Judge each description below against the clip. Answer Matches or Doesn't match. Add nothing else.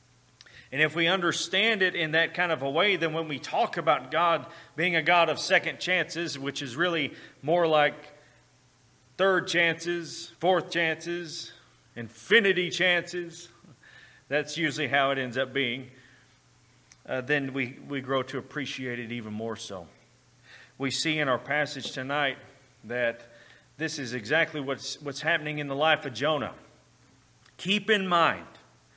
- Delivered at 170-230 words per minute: Doesn't match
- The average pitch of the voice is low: Doesn't match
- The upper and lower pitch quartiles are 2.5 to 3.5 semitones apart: Doesn't match